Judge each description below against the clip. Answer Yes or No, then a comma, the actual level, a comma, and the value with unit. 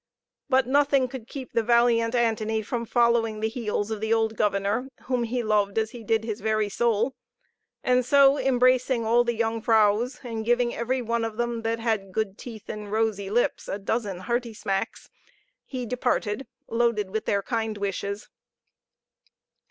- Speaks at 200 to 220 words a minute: No, average, 165 wpm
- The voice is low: No, high, 225 Hz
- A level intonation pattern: Yes, narrow, 2.1 semitones